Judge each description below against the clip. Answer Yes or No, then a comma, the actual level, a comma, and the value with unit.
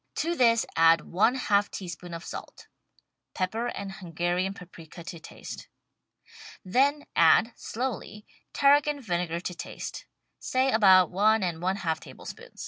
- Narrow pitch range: No, average, 5.0 semitones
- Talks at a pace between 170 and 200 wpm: No, average, 145 wpm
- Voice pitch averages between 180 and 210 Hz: Yes, high, 190 Hz